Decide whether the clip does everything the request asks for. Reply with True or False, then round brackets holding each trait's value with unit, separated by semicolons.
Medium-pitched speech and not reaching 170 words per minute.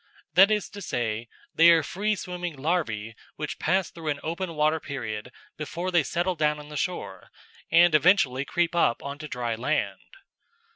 False (155 Hz; 175 wpm)